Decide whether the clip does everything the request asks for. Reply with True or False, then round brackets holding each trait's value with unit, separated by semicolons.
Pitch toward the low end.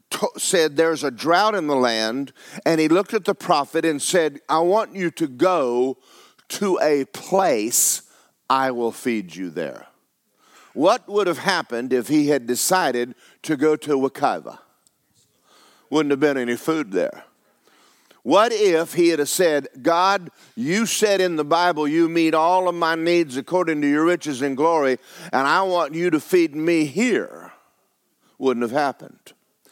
False (160 Hz)